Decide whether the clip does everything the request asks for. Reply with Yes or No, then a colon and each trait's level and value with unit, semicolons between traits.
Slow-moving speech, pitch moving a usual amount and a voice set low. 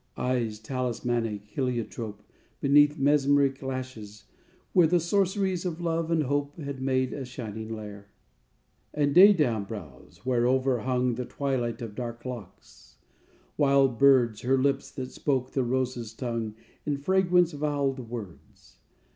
Yes: slow, 130 wpm; average, 3.5 semitones; low, 130 Hz